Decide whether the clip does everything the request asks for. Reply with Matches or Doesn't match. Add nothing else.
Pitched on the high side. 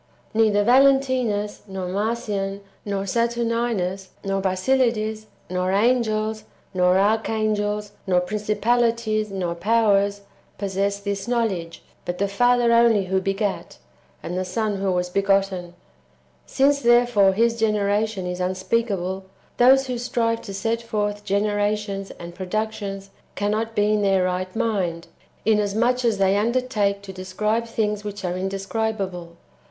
Matches